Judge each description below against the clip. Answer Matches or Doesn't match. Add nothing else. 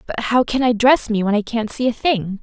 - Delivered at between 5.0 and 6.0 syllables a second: Matches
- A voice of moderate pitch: Doesn't match